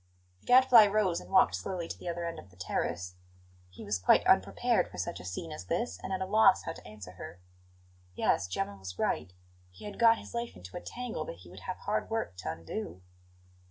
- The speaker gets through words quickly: Yes, fast, 225 wpm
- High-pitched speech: No, low, 105 Hz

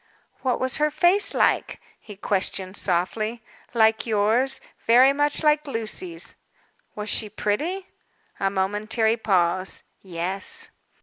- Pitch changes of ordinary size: No, wide, 6.6 semitones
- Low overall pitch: No, high, 220 Hz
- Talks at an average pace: No, slow, 115 wpm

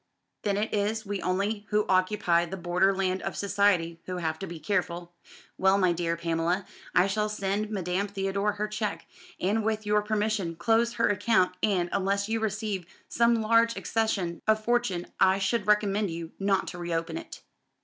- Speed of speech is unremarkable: Yes, average, 175 wpm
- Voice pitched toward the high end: Yes, high, 200 Hz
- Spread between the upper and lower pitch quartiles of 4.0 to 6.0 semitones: No, average, 2.9 semitones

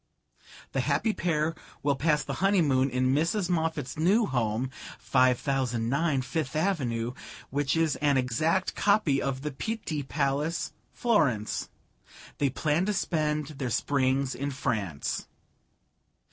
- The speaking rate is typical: No, slow, 120 wpm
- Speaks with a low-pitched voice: No, medium, 145 Hz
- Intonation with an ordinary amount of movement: Yes, average, 3.9 semitones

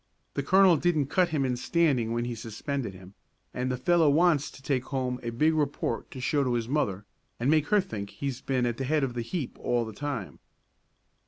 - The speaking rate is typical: No, fast, 220 wpm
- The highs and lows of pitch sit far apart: No, average, 4.3 semitones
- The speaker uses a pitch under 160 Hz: Yes, low, 135 Hz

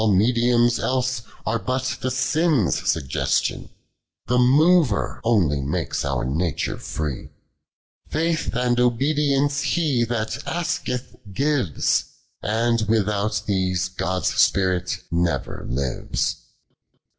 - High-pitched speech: No, low, 115 Hz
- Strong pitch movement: Yes, wide, 5.9 semitones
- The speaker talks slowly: Yes, slow, 100 wpm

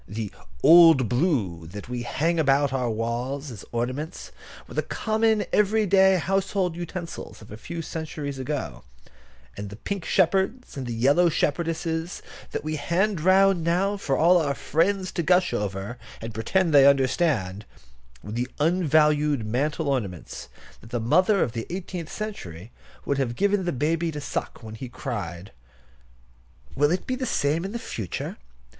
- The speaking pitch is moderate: Yes, medium, 150 Hz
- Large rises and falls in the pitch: Yes, wide, 7.0 semitones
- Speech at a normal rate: Yes, average, 160 wpm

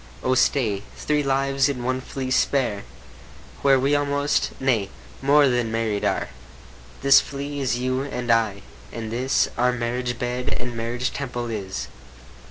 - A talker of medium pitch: No, low, 125 Hz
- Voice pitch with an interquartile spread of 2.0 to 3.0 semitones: Yes, average, 2.7 semitones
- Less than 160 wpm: Yes, average, 150 wpm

